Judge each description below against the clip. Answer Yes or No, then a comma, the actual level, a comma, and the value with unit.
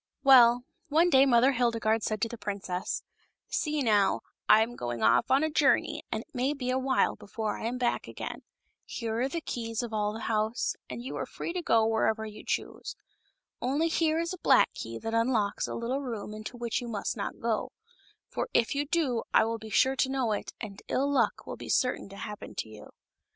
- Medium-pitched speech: No, high, 235 Hz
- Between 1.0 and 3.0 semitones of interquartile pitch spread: No, average, 3.6 semitones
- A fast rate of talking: Yes, fast, 220 wpm